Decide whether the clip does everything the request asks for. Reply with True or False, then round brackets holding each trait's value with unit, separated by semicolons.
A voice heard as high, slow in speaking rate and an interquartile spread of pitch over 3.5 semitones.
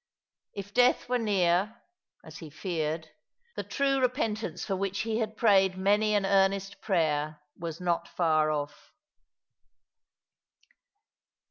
True (195 Hz; 120 wpm; 4.4 semitones)